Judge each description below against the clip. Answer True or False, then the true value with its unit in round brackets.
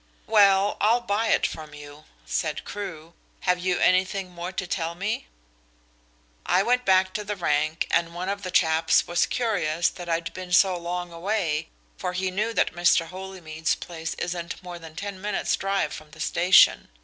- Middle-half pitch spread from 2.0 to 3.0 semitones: True (2.7 semitones)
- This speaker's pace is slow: False (175 wpm)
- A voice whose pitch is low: False (180 Hz)